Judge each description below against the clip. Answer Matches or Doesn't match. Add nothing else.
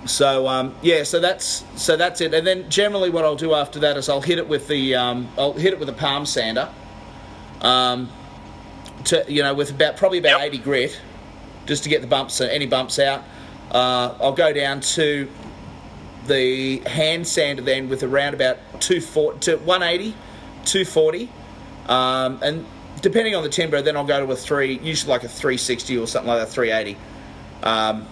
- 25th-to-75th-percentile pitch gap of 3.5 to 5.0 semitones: Matches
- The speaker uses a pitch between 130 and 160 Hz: Matches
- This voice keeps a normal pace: Matches